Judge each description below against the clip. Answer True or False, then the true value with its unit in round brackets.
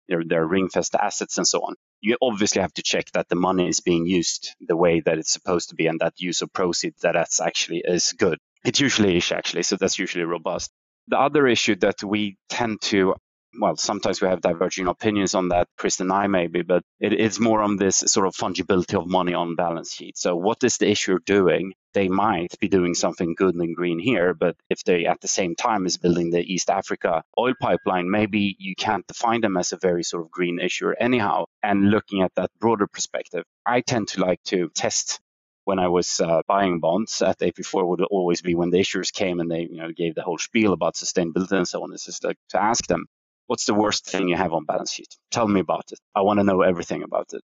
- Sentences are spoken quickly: True (230 wpm)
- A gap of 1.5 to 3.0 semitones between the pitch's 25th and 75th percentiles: True (2.4 semitones)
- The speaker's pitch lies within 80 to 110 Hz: True (95 Hz)